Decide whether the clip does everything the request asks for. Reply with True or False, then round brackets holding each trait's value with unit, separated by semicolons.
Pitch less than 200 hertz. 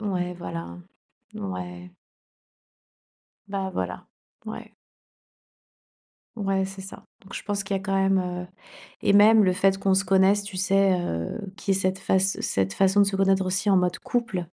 True (190 Hz)